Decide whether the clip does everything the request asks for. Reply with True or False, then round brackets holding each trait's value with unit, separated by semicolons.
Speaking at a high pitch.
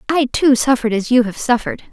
True (245 Hz)